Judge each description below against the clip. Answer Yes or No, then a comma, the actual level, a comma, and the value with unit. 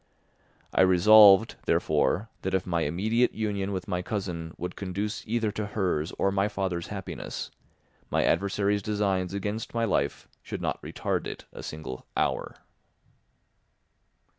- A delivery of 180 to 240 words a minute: No, average, 140 wpm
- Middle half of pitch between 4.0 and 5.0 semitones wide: No, narrow, 2.6 semitones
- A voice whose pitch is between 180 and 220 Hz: No, low, 100 Hz